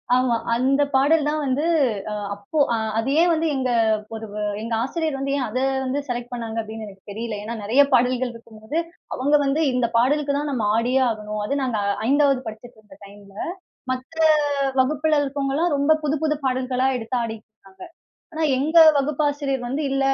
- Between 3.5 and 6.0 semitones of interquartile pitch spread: Yes, average, 3.9 semitones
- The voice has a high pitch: Yes, very high, 260 Hz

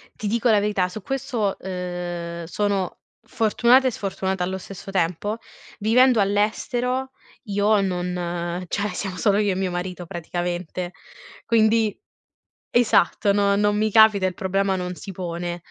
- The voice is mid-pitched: No, high, 195 Hz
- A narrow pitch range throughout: No, average, 3.1 semitones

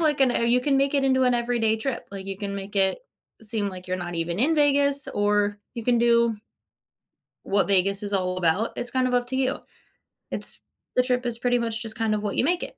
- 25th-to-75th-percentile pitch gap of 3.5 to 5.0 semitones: Yes, average, 4.1 semitones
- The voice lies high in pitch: Yes, high, 230 Hz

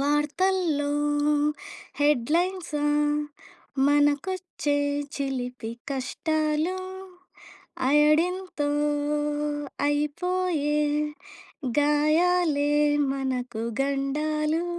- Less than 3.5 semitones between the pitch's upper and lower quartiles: Yes, average, 2.8 semitones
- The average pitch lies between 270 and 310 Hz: Yes, very high, 295 Hz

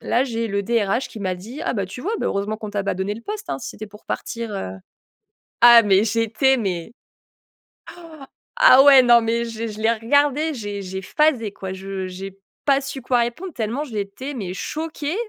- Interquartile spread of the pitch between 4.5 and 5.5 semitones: Yes, average, 4.8 semitones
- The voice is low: No, high, 225 Hz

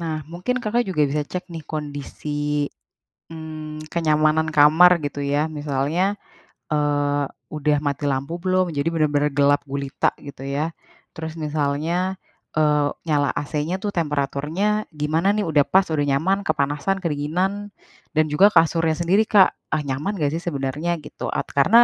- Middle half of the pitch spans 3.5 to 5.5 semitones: No, narrow, 2.6 semitones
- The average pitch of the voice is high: No, medium, 155 Hz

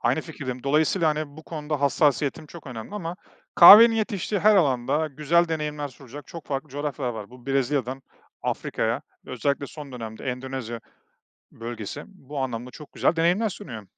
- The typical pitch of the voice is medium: Yes, medium, 145 Hz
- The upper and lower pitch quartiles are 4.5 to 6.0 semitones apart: No, average, 3.9 semitones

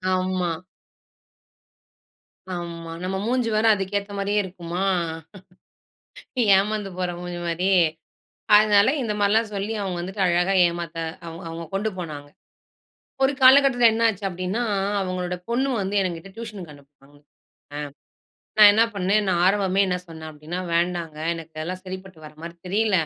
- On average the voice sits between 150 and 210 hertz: Yes, medium, 185 Hz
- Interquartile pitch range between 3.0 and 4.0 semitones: Yes, average, 3.3 semitones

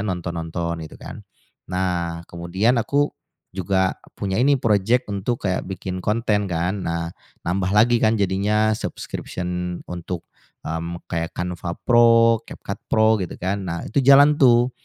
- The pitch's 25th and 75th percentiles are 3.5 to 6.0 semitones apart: Yes, average, 4.6 semitones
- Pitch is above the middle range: No, very low, 95 Hz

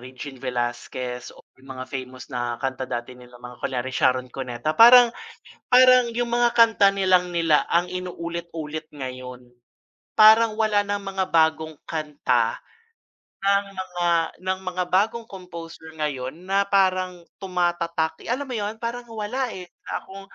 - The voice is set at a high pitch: No, medium, 175 Hz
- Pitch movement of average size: No, wide, 7.4 semitones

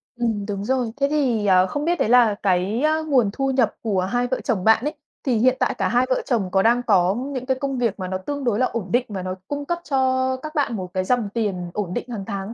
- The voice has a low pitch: No, high, 235 Hz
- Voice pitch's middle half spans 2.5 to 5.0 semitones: Yes, average, 4.7 semitones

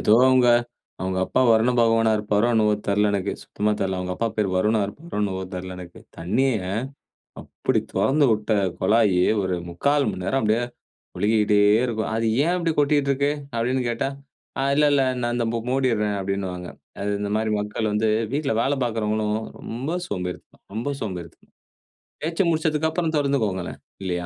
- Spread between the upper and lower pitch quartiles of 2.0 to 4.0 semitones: No, average, 4.8 semitones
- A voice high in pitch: No, low, 110 Hz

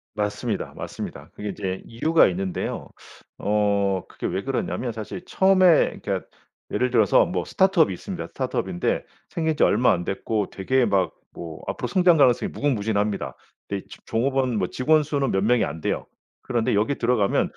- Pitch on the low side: Yes, low, 115 Hz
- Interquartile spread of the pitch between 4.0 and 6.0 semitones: Yes, wide, 5.6 semitones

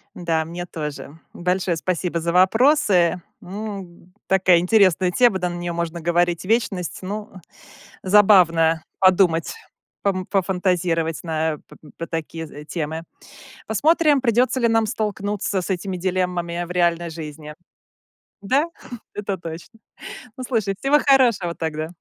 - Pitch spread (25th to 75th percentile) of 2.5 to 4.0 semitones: Yes, average, 3.3 semitones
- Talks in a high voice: No, medium, 180 Hz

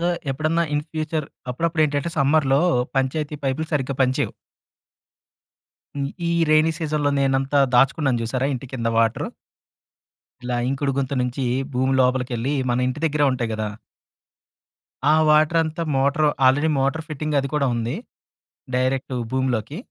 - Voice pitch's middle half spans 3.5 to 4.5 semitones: No, average, 2.9 semitones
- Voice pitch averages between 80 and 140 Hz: Yes, low, 135 Hz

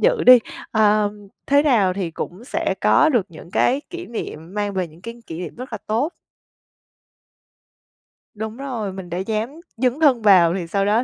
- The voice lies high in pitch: Yes, high, 215 Hz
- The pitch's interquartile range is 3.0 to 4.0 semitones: No, average, 5.0 semitones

